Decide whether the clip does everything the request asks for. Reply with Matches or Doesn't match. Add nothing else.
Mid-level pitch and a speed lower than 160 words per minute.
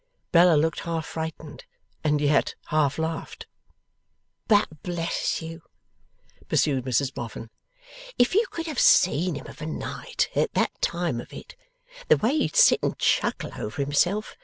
Matches